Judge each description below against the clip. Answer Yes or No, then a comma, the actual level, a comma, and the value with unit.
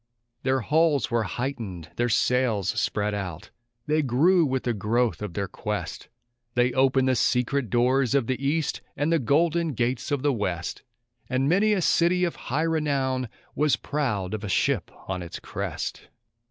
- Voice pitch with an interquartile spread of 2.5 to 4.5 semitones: No, average, 5.0 semitones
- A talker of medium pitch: No, low, 130 Hz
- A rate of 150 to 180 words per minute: Yes, average, 165 wpm